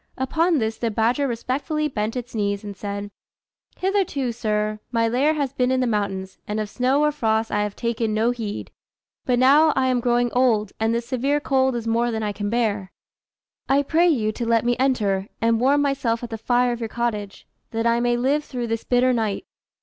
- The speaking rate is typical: No, fast, 210 wpm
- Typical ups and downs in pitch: Yes, average, 3.1 semitones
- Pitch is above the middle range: Yes, high, 235 Hz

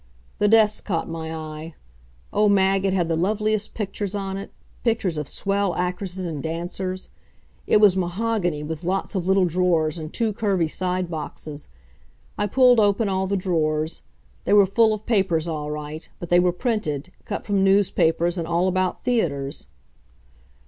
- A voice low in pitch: No, medium, 185 Hz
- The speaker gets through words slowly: No, average, 165 wpm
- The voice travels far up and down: No, average, 3.7 semitones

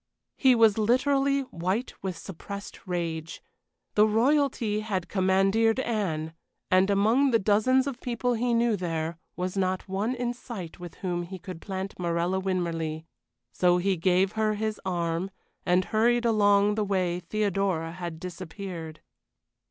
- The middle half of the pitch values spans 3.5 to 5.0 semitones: Yes, average, 4.0 semitones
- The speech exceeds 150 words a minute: No, average, 145 wpm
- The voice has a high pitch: Yes, high, 195 Hz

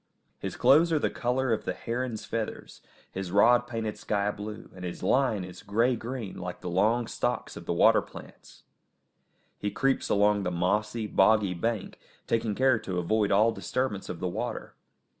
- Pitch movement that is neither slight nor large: Yes, average, 3.7 semitones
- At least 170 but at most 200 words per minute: Yes, average, 175 wpm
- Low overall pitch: Yes, low, 105 Hz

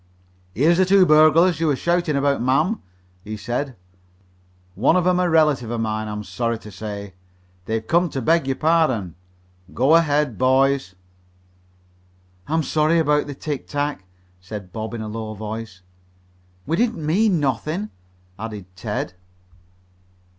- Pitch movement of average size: No, wide, 6.8 semitones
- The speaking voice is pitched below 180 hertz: Yes, medium, 140 Hz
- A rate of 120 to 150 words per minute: Yes, average, 140 wpm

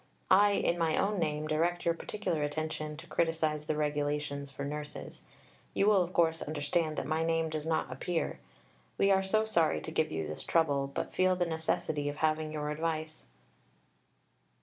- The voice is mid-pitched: Yes, medium, 155 Hz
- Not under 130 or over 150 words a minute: No, average, 175 wpm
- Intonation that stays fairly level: Yes, narrow, 2.2 semitones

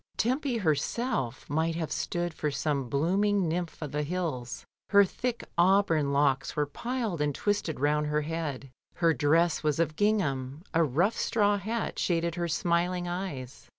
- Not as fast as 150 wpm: No, average, 155 wpm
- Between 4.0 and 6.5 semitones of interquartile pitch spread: Yes, average, 4.8 semitones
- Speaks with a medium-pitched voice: Yes, medium, 165 Hz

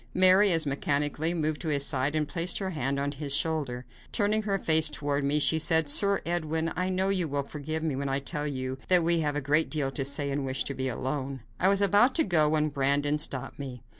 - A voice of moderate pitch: Yes, medium, 150 Hz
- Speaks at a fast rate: Yes, fast, 235 wpm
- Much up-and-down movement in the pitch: No, average, 3.1 semitones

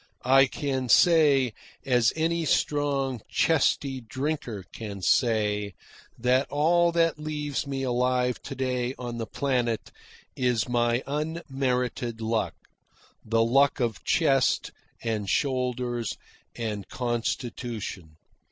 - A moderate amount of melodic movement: Yes, average, 3.3 semitones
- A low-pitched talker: Yes, low, 125 Hz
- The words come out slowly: Yes, slow, 105 wpm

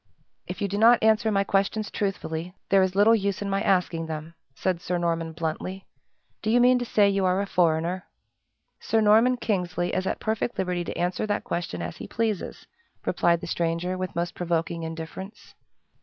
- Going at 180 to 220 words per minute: Yes, average, 185 wpm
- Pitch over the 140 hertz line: Yes, medium, 185 Hz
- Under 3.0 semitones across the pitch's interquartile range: No, average, 3.3 semitones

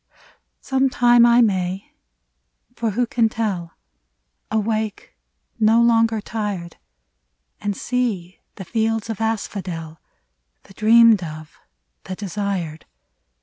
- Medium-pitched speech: No, high, 210 Hz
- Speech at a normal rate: No, slow, 105 wpm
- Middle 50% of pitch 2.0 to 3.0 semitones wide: No, average, 4.2 semitones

